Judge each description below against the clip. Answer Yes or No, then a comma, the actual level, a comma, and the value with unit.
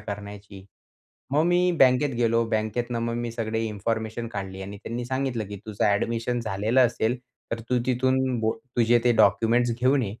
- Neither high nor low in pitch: No, low, 115 Hz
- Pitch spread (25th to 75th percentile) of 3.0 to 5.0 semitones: No, narrow, 2.4 semitones